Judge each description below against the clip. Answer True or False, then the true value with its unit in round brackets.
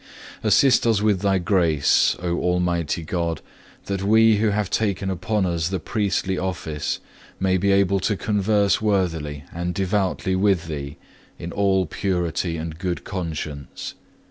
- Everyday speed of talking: True (145 wpm)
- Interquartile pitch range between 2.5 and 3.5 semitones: True (2.9 semitones)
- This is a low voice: True (95 Hz)